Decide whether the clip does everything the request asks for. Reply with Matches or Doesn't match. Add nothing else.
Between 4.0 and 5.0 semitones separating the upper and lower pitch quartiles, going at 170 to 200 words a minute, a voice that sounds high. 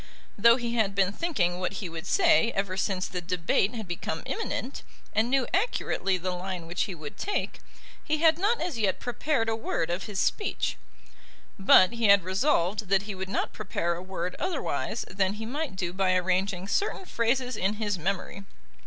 Matches